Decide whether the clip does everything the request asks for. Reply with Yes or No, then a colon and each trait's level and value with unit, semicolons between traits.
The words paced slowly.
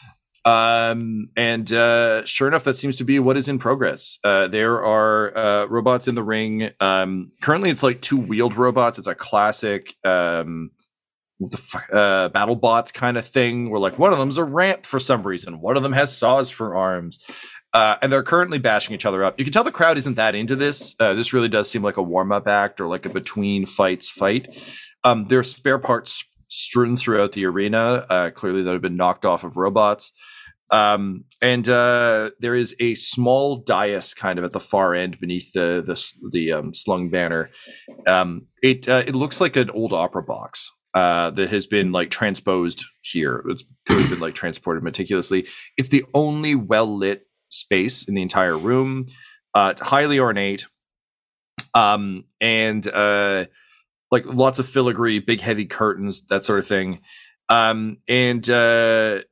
No: average, 180 wpm